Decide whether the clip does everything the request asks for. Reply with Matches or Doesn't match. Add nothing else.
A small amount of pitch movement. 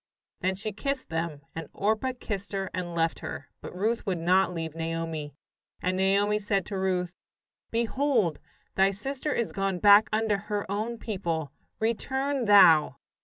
Doesn't match